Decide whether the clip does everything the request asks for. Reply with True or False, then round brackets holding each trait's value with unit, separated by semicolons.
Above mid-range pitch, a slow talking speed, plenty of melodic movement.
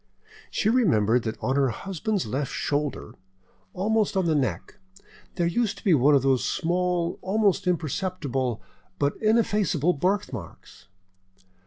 False (170 Hz; 130 wpm; 6.4 semitones)